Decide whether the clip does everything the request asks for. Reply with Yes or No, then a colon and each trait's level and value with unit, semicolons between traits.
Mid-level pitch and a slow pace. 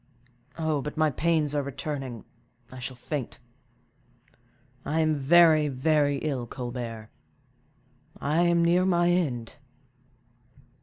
Yes: medium, 150 Hz; slow, 105 wpm